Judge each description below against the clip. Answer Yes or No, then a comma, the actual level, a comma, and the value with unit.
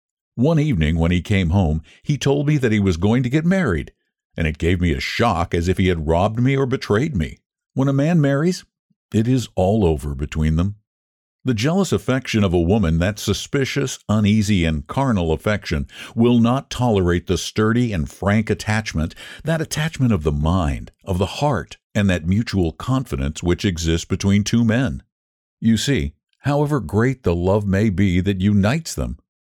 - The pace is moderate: Yes, average, 180 wpm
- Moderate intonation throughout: No, wide, 6.6 semitones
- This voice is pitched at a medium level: No, low, 105 Hz